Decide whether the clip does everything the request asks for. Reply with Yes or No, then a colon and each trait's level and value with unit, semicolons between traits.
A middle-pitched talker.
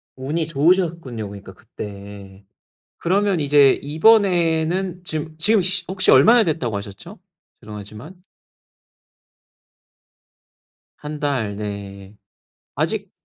Yes: medium, 150 Hz